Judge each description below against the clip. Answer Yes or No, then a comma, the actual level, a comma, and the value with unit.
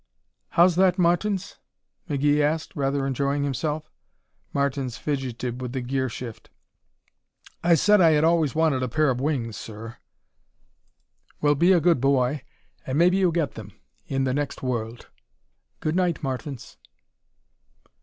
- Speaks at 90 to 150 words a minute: Yes, average, 140 wpm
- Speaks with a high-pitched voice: No, medium, 145 Hz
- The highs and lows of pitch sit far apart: No, average, 4.0 semitones